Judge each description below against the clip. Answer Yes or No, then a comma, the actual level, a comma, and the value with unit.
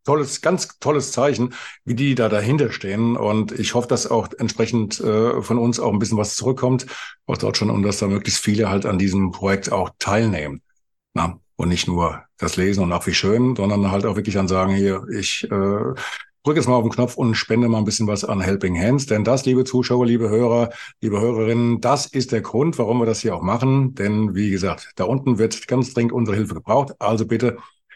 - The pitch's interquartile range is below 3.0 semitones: No, average, 3.6 semitones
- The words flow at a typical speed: No, fast, 220 wpm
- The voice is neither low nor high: No, low, 110 Hz